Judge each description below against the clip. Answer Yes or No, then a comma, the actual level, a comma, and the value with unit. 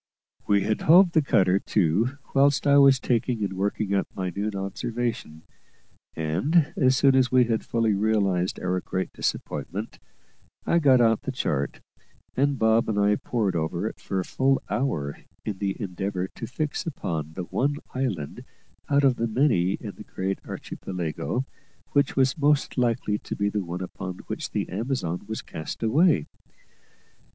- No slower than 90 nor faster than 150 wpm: No, average, 165 wpm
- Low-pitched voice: Yes, low, 110 Hz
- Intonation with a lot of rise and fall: Yes, wide, 6.1 semitones